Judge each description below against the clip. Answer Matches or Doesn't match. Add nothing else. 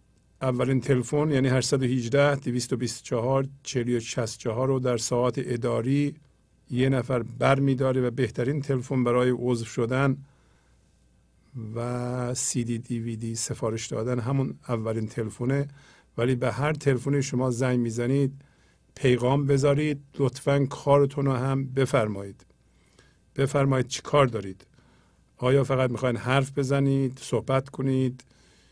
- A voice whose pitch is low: Matches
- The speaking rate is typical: Doesn't match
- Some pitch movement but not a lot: Doesn't match